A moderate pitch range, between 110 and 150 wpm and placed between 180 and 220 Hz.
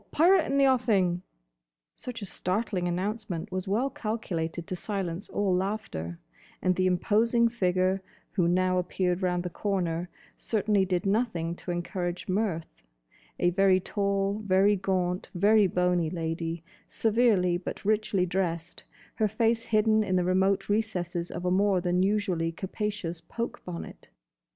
Yes: average, 3.1 semitones; average, 140 wpm; medium, 185 Hz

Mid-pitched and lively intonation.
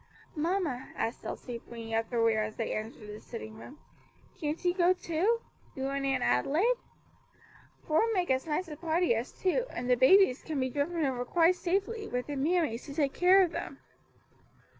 No: very high, 290 Hz; wide, 6.5 semitones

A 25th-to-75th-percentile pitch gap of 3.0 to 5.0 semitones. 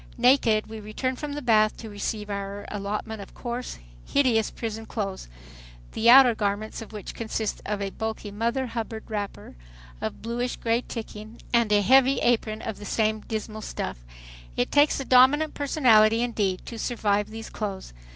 No: narrow, 2.5 semitones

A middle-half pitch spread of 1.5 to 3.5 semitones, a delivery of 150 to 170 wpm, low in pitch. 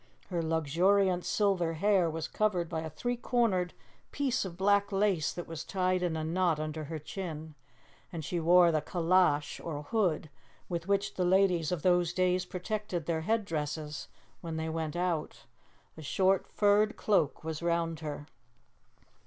No: average, 3.2 semitones; average, 160 wpm; medium, 175 Hz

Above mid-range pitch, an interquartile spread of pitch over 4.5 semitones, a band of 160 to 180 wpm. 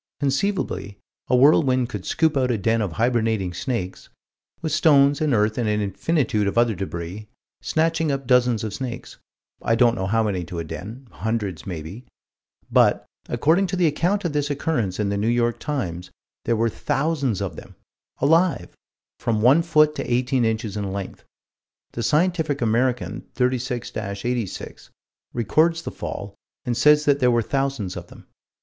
No: low, 120 Hz; wide, 5.4 semitones; average, 165 wpm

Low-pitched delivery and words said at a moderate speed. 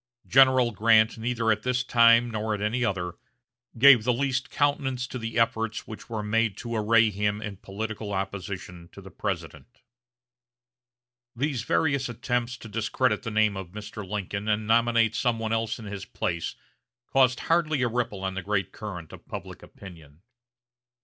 Yes: low, 110 Hz; average, 165 wpm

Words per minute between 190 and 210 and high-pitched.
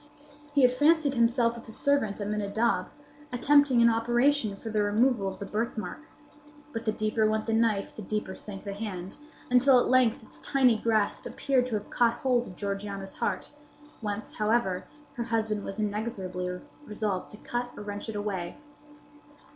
No: average, 170 wpm; high, 220 Hz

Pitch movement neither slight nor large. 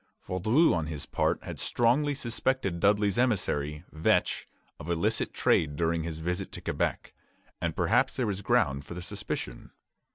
No: wide, 6.4 semitones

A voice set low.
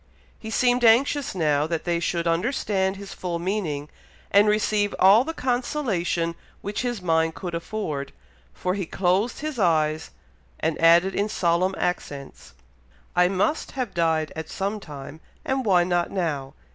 No: medium, 180 Hz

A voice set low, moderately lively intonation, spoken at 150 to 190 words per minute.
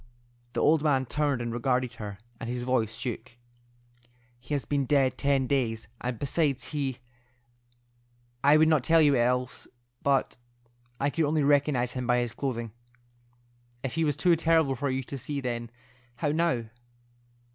Yes: low, 130 Hz; average, 3.0 semitones; average, 155 wpm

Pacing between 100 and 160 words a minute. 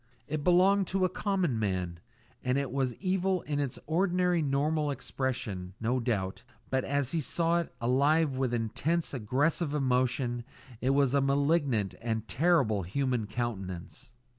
Yes: average, 145 wpm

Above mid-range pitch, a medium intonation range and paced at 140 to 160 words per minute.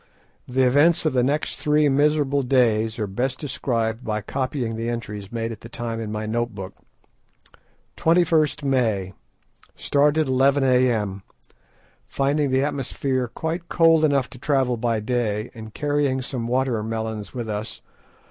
No: low, 125 Hz; average, 4.0 semitones; average, 145 wpm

